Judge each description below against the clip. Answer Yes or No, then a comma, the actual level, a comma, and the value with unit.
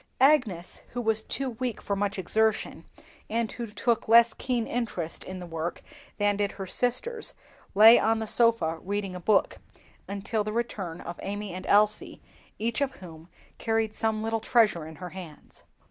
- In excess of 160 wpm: Yes, average, 170 wpm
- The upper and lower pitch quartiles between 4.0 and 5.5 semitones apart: No, average, 3.6 semitones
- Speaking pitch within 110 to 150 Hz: No, high, 215 Hz